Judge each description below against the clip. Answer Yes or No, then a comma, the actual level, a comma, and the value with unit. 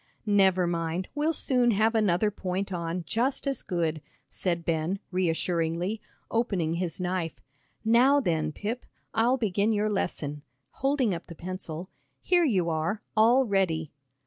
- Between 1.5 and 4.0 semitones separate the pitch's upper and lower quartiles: No, average, 4.9 semitones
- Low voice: No, medium, 185 Hz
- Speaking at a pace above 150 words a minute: No, average, 140 wpm